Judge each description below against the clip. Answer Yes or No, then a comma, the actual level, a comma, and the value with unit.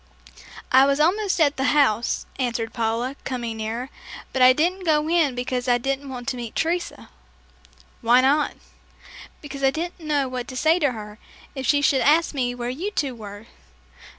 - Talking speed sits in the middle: Yes, average, 180 wpm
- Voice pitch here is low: No, very high, 265 Hz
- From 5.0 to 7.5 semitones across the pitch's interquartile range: No, average, 3.6 semitones